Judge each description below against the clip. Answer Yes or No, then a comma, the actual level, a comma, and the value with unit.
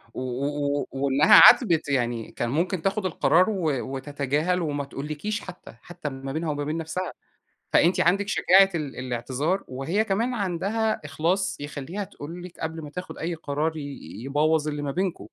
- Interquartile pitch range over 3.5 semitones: Yes, average, 4.5 semitones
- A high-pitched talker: No, medium, 160 Hz